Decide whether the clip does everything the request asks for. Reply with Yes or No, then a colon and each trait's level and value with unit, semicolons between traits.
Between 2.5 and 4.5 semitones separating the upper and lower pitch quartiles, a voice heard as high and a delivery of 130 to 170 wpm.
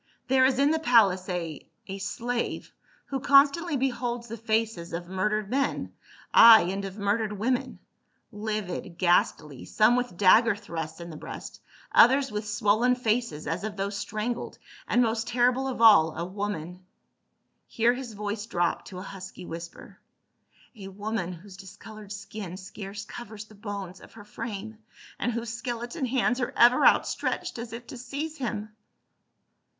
Yes: average, 3.9 semitones; high, 215 Hz; average, 165 wpm